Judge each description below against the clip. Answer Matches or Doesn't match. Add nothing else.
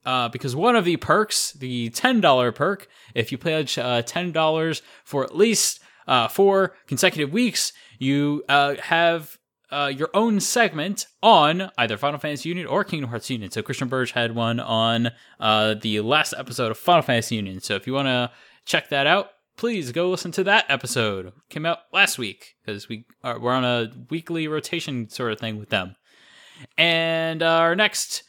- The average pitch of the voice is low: Doesn't match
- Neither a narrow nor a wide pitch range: Doesn't match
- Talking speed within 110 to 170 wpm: Doesn't match